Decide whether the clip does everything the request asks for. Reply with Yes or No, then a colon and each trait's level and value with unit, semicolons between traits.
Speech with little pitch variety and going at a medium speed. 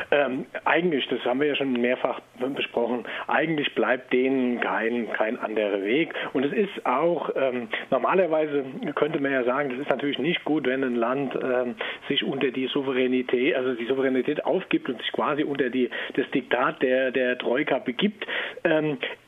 Yes: narrow, 2.1 semitones; average, 170 wpm